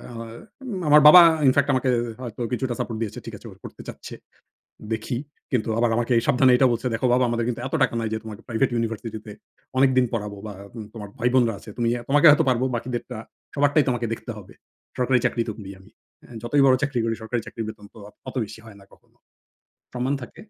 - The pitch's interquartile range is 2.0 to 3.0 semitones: Yes, narrow, 2.5 semitones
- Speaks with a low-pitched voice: Yes, low, 120 Hz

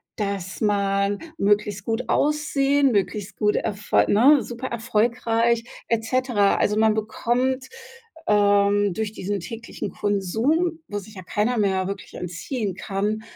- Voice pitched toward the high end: Yes, high, 210 Hz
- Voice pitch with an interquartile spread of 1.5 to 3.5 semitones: Yes, average, 2.9 semitones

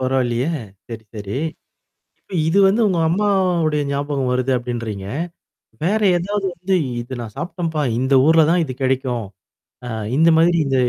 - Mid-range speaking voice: Yes, medium, 145 Hz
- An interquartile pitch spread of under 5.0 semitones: No, wide, 5.6 semitones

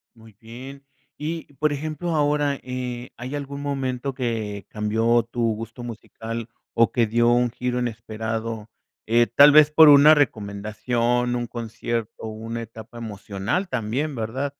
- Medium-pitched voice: No, low, 120 Hz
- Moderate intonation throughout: Yes, average, 3.6 semitones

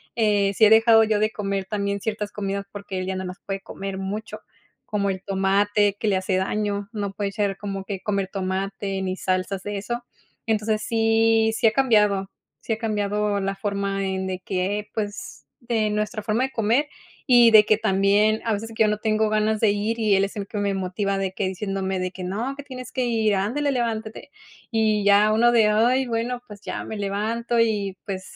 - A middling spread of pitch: No, narrow, 2.1 semitones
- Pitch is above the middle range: Yes, high, 210 Hz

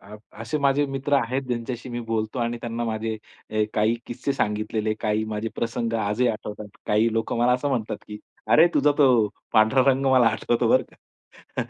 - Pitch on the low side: Yes, low, 115 Hz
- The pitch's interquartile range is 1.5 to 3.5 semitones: Yes, average, 2.7 semitones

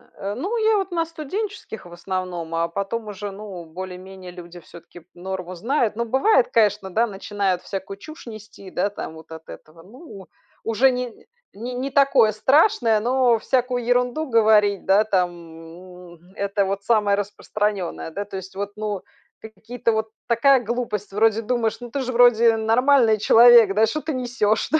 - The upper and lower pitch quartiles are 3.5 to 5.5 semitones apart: Yes, average, 4.4 semitones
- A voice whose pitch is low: No, high, 215 Hz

